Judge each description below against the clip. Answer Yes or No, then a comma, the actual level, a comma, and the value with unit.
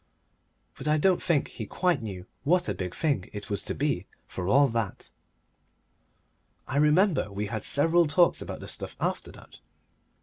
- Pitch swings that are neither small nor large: No, wide, 8.1 semitones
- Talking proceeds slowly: No, average, 170 wpm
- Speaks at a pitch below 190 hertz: Yes, medium, 140 Hz